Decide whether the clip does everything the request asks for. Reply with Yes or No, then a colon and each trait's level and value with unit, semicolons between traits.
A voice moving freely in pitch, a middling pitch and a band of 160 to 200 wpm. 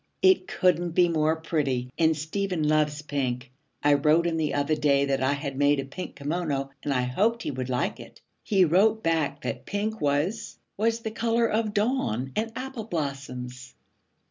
Yes: wide, 6.4 semitones; medium, 155 Hz; average, 180 wpm